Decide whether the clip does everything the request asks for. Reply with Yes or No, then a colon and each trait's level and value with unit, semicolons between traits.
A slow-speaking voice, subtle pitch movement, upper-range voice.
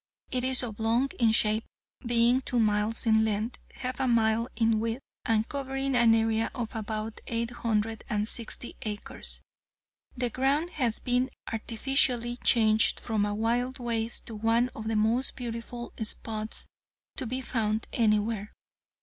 No: average, 150 wpm; narrow, 2.0 semitones; high, 230 Hz